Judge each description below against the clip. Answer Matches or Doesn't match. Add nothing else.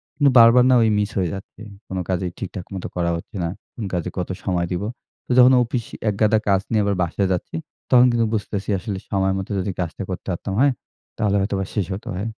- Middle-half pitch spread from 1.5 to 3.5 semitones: Matches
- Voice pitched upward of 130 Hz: Doesn't match